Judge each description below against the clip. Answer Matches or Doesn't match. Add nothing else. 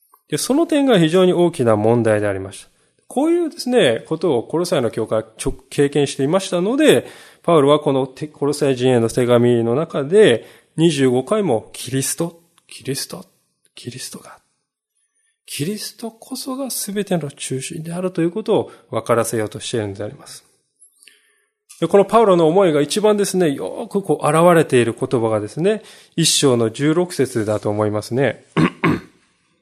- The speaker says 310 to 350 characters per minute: Matches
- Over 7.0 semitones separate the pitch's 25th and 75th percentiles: Matches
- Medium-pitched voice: Matches